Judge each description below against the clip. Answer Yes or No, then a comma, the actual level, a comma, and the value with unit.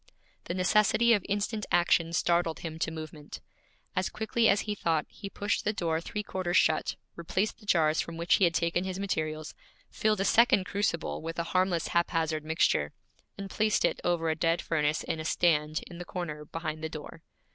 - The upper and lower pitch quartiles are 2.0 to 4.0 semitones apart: Yes, average, 3.5 semitones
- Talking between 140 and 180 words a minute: No, average, 190 wpm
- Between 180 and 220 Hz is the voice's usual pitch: No, medium, 170 Hz